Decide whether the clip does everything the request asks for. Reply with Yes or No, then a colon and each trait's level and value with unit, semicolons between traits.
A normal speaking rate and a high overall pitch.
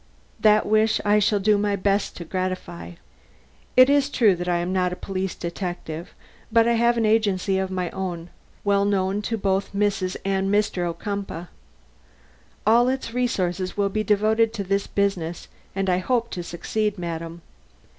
Yes: average, 165 wpm; high, 195 Hz